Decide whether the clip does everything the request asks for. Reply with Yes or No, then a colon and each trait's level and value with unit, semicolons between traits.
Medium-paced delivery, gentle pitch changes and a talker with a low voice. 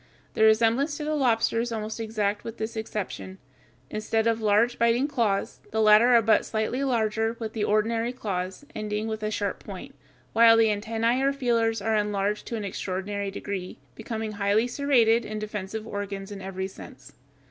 No: average, 175 wpm; narrow, 1.9 semitones; high, 220 Hz